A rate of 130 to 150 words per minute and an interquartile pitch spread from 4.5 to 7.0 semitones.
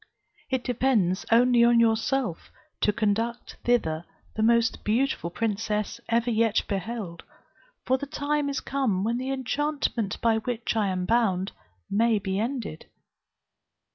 No: slow, 135 wpm; average, 3.2 semitones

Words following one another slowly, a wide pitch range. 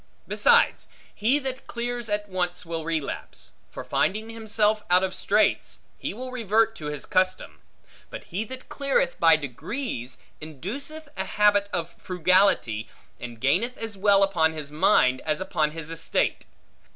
No: average, 150 wpm; wide, 5.9 semitones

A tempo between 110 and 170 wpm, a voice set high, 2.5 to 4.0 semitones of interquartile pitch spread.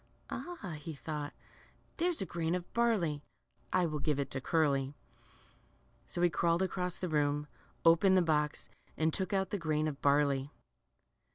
No: average, 160 wpm; medium, 160 Hz; average, 3.6 semitones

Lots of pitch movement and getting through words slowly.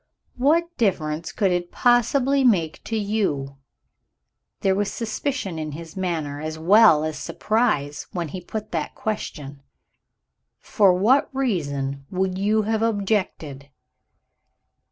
Yes: wide, 6.1 semitones; slow, 120 wpm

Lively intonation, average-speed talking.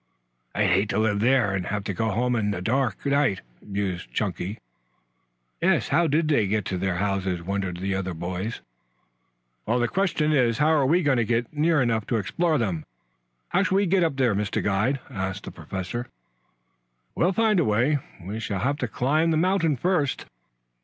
Yes: wide, 7.1 semitones; average, 185 wpm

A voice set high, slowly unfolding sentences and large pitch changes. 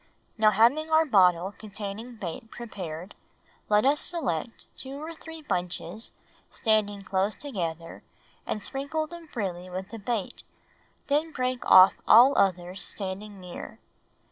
Yes: high, 215 Hz; slow, 130 wpm; wide, 6.2 semitones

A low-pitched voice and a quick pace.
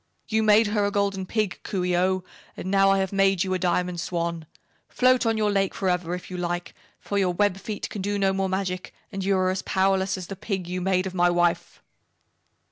No: high, 190 Hz; fast, 225 wpm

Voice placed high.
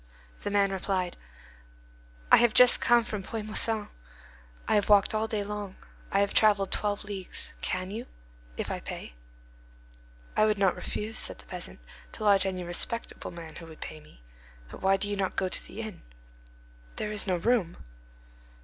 Yes: high, 200 Hz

